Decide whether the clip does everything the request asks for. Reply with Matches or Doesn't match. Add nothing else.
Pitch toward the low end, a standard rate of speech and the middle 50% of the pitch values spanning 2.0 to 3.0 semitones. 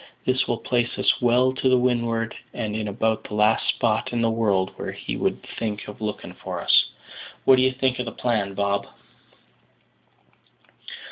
Matches